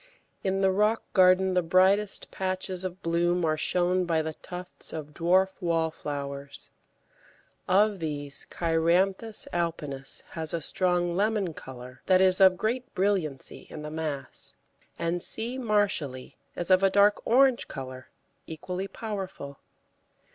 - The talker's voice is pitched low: No, medium, 180 Hz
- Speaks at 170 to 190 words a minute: No, slow, 135 wpm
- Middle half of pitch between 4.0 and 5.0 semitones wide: No, average, 3.4 semitones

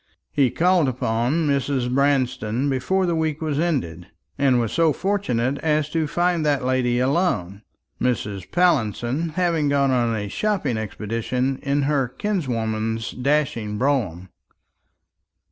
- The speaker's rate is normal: No, slow, 130 wpm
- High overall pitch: No, low, 135 Hz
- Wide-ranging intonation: No, average, 5.0 semitones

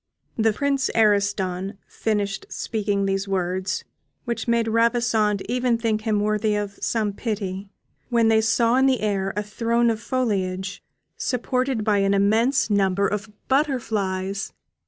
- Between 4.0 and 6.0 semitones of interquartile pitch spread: No, average, 2.7 semitones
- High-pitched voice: Yes, high, 215 Hz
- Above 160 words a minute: No, slow, 135 wpm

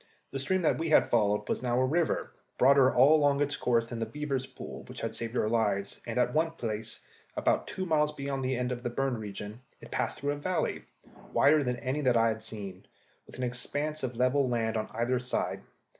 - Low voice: Yes, low, 125 Hz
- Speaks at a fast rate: Yes, fast, 220 wpm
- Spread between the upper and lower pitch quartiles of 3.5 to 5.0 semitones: Yes, average, 3.8 semitones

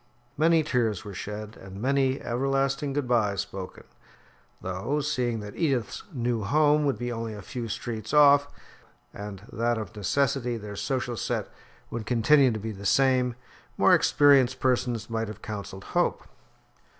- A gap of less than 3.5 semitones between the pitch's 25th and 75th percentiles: No, average, 4.2 semitones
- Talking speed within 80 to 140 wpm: No, average, 150 wpm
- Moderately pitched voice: No, low, 120 Hz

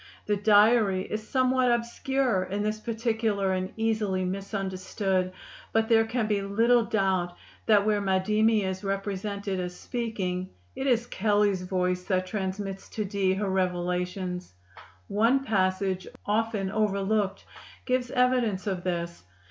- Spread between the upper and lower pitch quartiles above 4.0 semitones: No, average, 2.9 semitones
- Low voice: No, high, 200 Hz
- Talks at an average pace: No, slow, 130 wpm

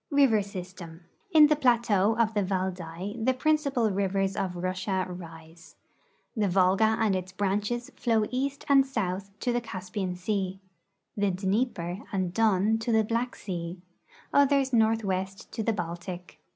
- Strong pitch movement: No, average, 4.0 semitones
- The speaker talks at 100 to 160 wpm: Yes, average, 145 wpm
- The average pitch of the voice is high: Yes, high, 200 Hz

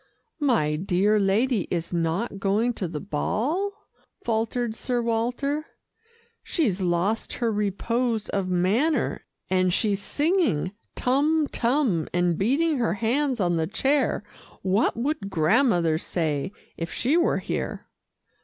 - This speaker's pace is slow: Yes, slow, 125 wpm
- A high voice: Yes, high, 220 Hz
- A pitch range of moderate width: No, wide, 6.1 semitones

